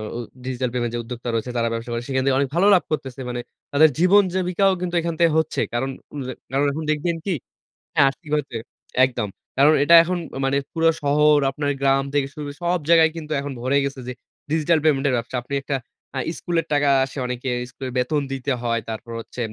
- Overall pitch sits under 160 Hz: Yes, medium, 140 Hz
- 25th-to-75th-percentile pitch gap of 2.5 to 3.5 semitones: No, average, 3.9 semitones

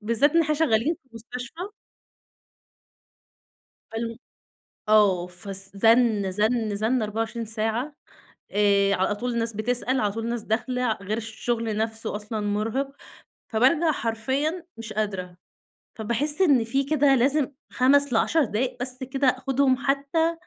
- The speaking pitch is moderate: No, high, 230 Hz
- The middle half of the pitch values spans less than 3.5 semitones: No, average, 3.8 semitones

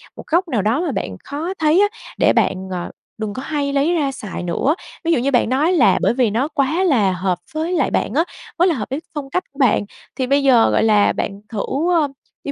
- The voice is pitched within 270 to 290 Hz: Yes, very high, 275 Hz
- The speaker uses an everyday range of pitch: No, wide, 6.1 semitones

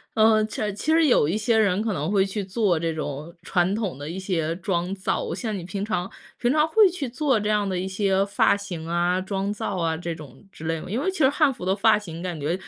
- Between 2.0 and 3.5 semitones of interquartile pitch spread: No, average, 4.1 semitones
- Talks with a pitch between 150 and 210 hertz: Yes, high, 195 Hz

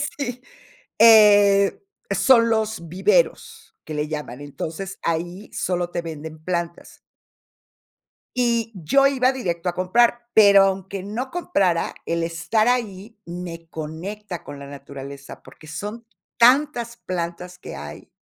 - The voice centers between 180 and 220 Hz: Yes, high, 190 Hz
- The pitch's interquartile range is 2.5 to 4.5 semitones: No, wide, 5.6 semitones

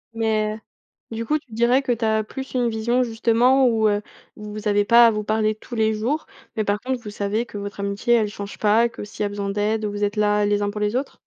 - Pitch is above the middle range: Yes, high, 220 Hz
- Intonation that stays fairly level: Yes, narrow, 2.3 semitones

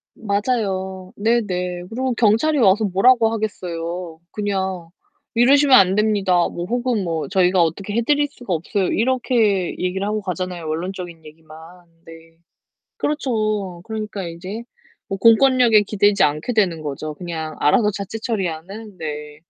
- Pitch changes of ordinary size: Yes, average, 4.3 semitones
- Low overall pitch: No, high, 195 Hz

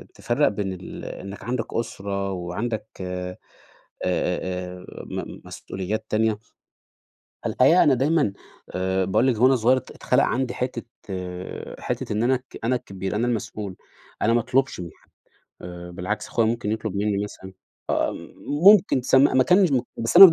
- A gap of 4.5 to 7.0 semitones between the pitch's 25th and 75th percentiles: Yes, average, 5.1 semitones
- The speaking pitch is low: Yes, low, 110 Hz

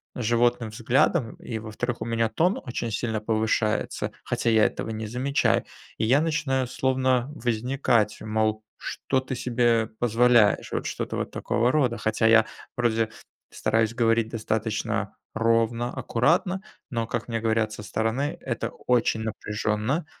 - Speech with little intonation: Yes, narrow, 2.2 semitones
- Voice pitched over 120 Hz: No, low, 115 Hz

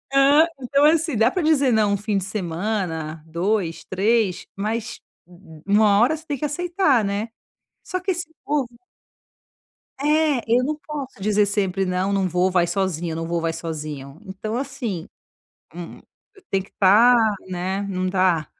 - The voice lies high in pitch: Yes, high, 205 Hz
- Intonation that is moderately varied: No, wide, 6.8 semitones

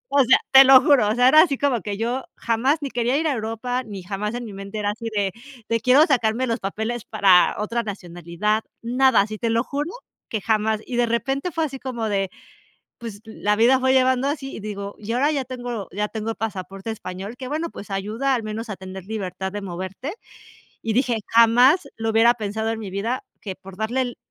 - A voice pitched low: No, high, 225 Hz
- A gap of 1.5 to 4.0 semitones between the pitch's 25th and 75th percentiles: Yes, average, 3.7 semitones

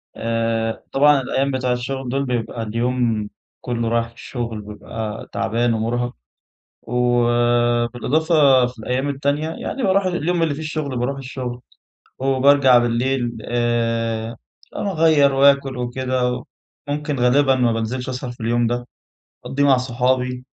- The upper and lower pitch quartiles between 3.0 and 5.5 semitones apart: No, narrow, 2.5 semitones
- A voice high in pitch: No, low, 125 Hz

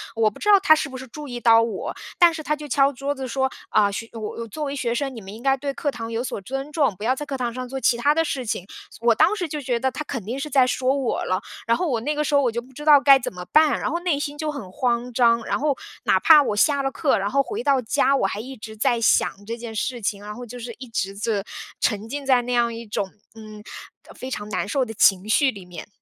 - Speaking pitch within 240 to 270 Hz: Yes, very high, 250 Hz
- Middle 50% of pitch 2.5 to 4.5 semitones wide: Yes, average, 3.9 semitones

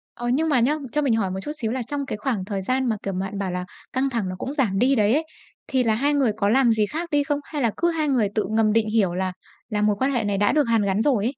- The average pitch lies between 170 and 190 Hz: No, high, 230 Hz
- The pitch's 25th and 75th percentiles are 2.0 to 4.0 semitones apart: No, average, 4.9 semitones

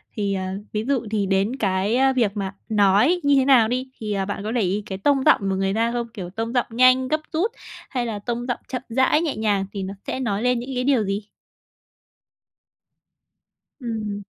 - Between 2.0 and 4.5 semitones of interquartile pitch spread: Yes, average, 4.2 semitones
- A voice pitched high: Yes, high, 225 Hz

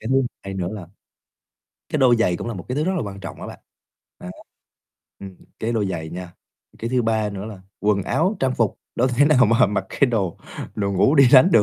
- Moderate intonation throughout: Yes, average, 4.8 semitones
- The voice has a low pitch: Yes, low, 110 Hz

